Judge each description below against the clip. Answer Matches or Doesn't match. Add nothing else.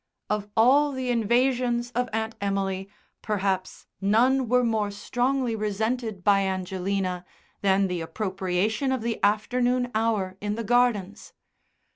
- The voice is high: Matches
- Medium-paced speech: Doesn't match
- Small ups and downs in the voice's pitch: Doesn't match